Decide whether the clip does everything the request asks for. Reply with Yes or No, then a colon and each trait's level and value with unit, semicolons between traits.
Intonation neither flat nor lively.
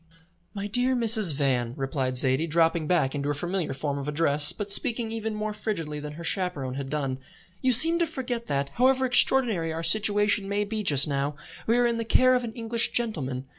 No: wide, 7.9 semitones